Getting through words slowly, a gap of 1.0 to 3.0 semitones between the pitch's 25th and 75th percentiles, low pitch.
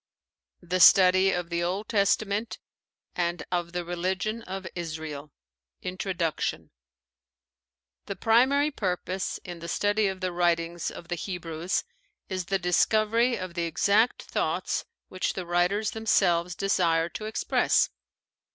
No: slow, 125 wpm; average, 2.7 semitones; medium, 185 Hz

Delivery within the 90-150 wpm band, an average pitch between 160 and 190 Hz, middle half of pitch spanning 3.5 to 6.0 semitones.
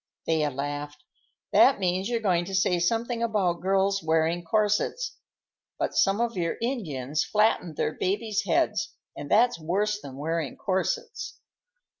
Yes: average, 140 wpm; medium, 185 Hz; average, 4.9 semitones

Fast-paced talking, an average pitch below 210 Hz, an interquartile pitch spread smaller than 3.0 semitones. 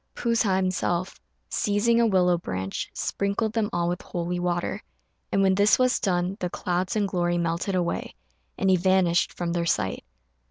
No: average, 170 wpm; medium, 185 Hz; narrow, 2.4 semitones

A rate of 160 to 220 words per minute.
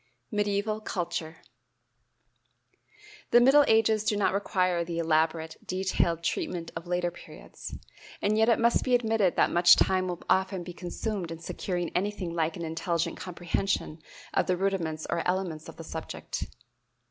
No: average, 150 wpm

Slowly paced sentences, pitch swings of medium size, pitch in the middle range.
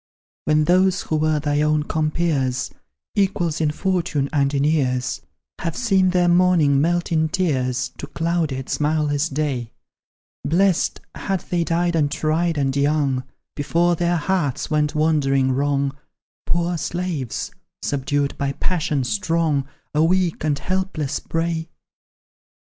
Yes: slow, 125 wpm; average, 3.4 semitones; medium, 155 Hz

